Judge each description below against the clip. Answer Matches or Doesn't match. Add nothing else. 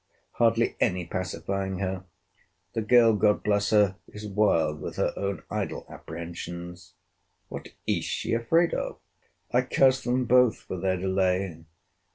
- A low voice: Matches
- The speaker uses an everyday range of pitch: Matches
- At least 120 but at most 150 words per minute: Matches